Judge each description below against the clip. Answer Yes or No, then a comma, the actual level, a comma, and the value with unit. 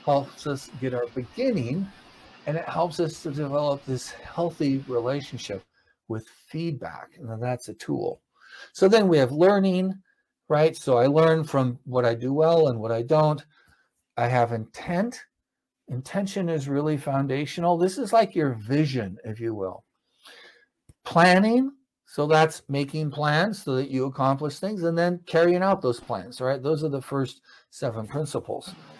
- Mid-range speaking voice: Yes, medium, 150 Hz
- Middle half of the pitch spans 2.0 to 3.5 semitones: No, average, 4.8 semitones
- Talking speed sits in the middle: Yes, average, 160 wpm